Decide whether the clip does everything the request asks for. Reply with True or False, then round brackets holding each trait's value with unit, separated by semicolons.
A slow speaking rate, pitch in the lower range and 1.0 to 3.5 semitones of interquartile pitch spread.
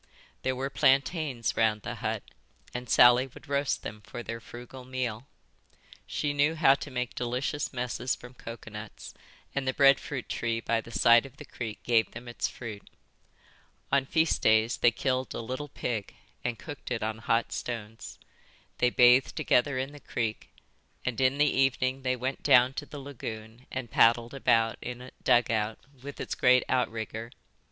False (170 wpm; 125 Hz; 2.5 semitones)